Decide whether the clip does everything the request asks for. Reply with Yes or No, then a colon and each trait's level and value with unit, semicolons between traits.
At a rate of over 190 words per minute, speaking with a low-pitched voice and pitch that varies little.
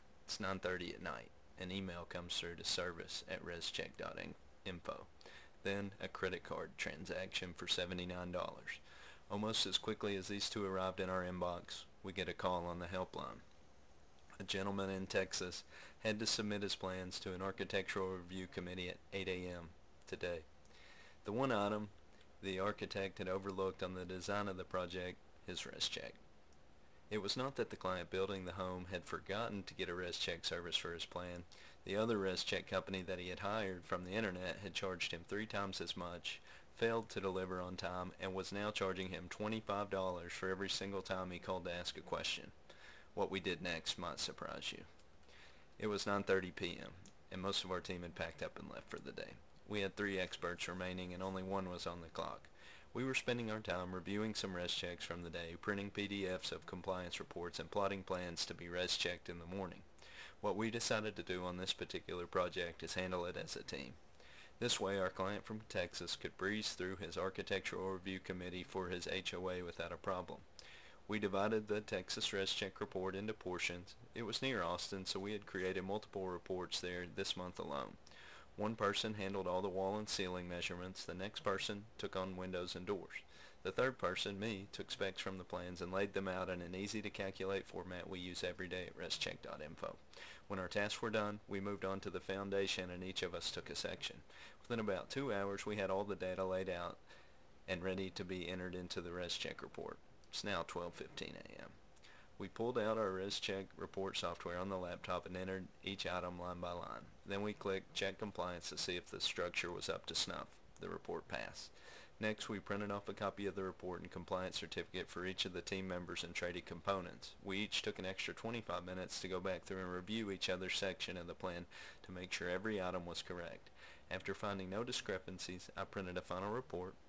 Yes: average, 200 wpm; very low, 95 Hz; narrow, 1.8 semitones